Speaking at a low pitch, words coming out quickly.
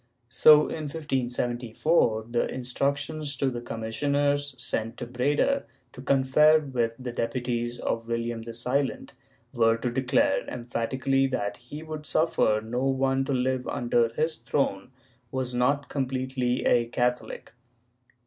No: low, 130 Hz; average, 140 wpm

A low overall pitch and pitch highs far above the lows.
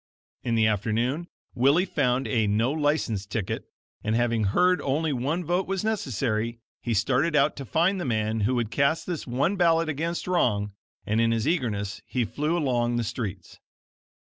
Yes: low, 125 Hz; wide, 6.3 semitones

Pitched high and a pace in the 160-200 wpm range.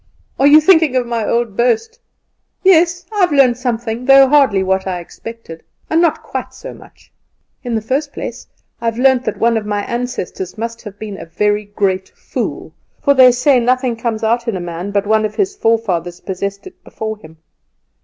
Yes: high, 230 Hz; average, 195 wpm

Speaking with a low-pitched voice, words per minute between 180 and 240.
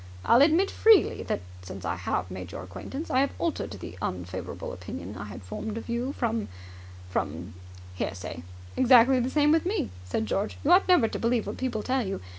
No: high, 225 Hz; average, 200 wpm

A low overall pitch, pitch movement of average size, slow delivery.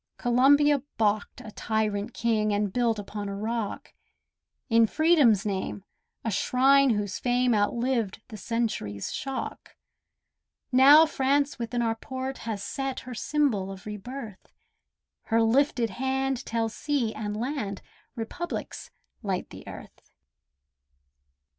No: high, 230 Hz; average, 4.1 semitones; slow, 120 wpm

